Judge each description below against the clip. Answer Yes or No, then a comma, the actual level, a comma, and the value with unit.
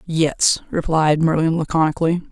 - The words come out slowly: Yes, slow, 105 wpm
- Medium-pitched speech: Yes, medium, 160 Hz